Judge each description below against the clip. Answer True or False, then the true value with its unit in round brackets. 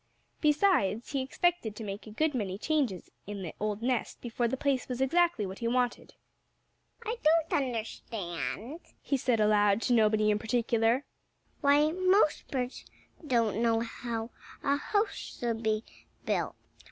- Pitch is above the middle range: True (235 Hz)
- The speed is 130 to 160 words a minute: True (150 wpm)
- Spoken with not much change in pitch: False (4.9 semitones)